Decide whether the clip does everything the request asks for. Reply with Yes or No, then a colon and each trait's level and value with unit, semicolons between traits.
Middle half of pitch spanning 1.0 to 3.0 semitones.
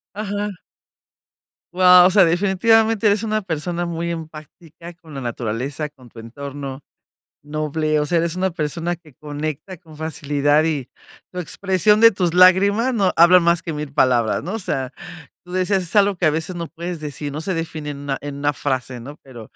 No: average, 4.0 semitones